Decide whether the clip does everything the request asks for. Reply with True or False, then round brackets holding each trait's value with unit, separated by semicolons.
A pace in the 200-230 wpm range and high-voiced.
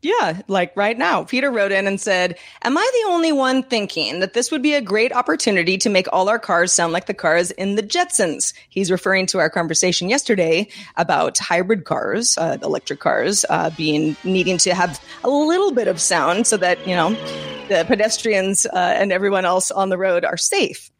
True (205 wpm; 195 Hz)